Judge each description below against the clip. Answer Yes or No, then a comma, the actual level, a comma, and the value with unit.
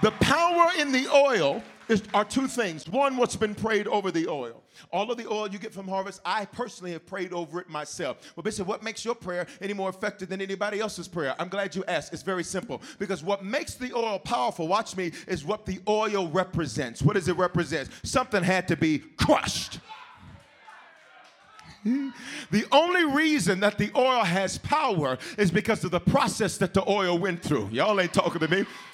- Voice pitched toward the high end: Yes, high, 200 Hz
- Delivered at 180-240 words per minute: Yes, average, 200 wpm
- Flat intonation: No, average, 3.7 semitones